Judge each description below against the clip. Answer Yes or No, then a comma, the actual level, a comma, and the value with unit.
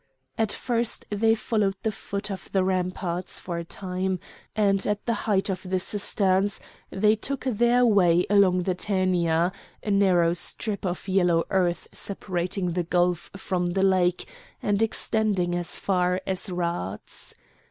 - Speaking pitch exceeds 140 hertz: Yes, high, 190 Hz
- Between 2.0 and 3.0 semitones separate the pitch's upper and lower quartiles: Yes, narrow, 2.5 semitones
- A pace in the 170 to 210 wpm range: No, average, 150 wpm